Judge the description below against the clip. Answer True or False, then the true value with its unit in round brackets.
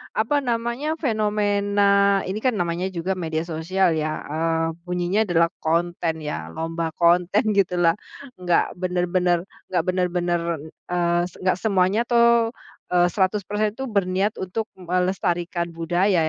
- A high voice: False (180 Hz)